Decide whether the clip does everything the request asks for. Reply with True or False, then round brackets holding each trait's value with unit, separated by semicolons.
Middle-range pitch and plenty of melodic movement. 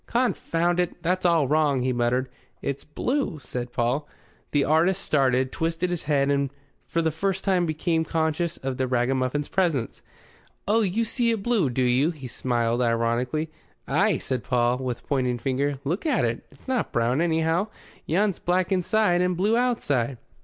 True (155 Hz; 5.7 semitones)